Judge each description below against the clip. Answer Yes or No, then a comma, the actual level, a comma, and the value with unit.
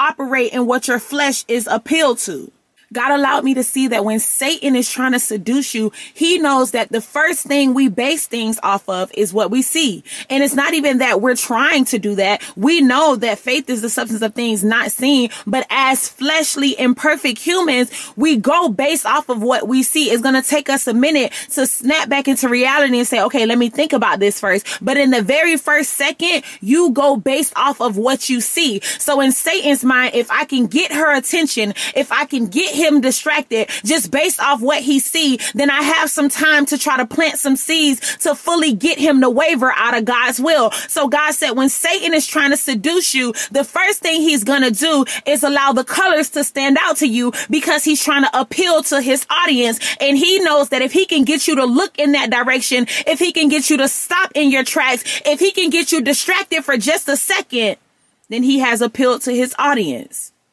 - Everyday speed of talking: No, fast, 220 wpm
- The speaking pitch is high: Yes, very high, 275 Hz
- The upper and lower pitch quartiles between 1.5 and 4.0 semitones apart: Yes, average, 3.4 semitones